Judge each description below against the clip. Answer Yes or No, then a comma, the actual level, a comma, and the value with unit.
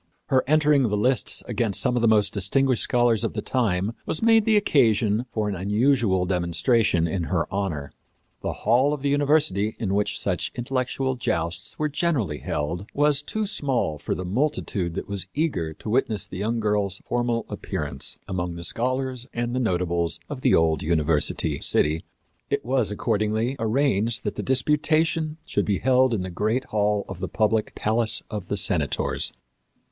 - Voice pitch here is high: No, low, 110 Hz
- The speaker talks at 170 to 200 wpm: Yes, average, 175 wpm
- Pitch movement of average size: No, wide, 5.7 semitones